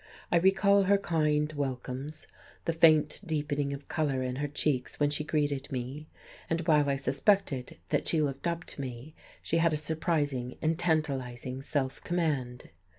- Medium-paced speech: Yes, average, 160 wpm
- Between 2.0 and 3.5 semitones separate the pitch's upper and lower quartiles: Yes, average, 3.2 semitones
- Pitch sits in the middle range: Yes, medium, 150 Hz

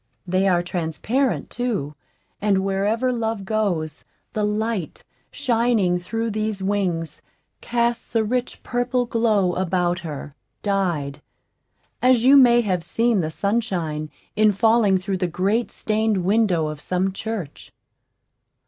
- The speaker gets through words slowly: Yes, slow, 125 wpm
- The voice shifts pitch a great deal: No, average, 4.3 semitones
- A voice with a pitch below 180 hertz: No, high, 200 Hz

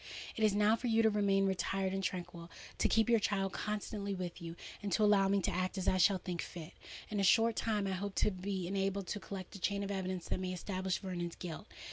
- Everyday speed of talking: No, fast, 230 wpm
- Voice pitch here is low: No, high, 195 Hz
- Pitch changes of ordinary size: No, narrow, 1.9 semitones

